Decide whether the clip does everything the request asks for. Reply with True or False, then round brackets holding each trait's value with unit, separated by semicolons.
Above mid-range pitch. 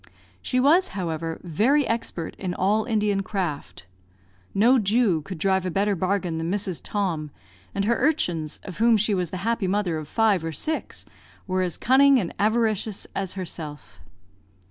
True (195 Hz)